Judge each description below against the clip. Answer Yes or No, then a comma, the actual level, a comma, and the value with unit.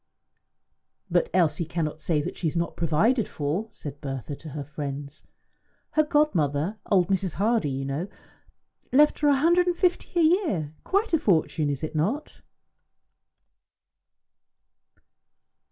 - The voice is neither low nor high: Yes, medium, 170 Hz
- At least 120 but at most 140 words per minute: Yes, slow, 135 wpm